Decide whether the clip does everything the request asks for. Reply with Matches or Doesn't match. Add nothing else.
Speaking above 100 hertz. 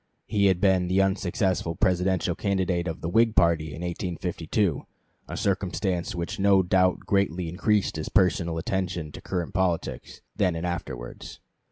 Doesn't match